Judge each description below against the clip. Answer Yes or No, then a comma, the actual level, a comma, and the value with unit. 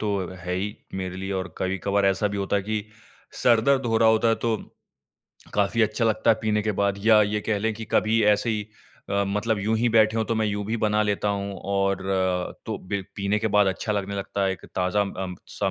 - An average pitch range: No, narrow, 1.9 semitones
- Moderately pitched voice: No, low, 105 Hz